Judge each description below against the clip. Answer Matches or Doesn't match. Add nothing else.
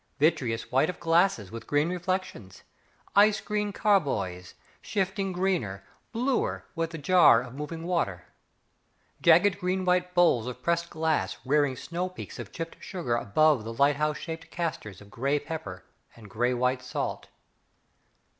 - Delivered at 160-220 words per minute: Doesn't match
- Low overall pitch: Doesn't match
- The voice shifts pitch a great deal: Matches